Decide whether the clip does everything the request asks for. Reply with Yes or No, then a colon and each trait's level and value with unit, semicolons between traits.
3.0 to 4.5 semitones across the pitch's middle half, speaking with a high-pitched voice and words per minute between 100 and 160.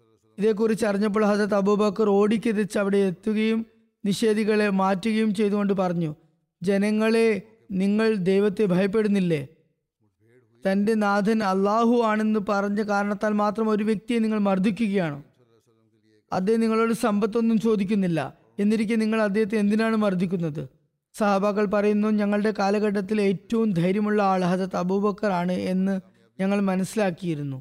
No: narrow, 2.5 semitones; high, 205 Hz; average, 105 wpm